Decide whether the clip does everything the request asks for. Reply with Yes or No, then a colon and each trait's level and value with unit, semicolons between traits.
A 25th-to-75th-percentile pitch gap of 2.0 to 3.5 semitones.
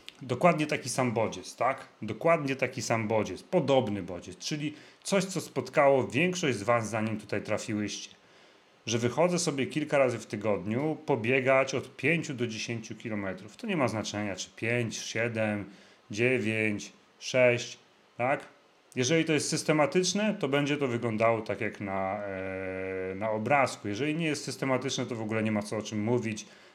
No: average, 4.7 semitones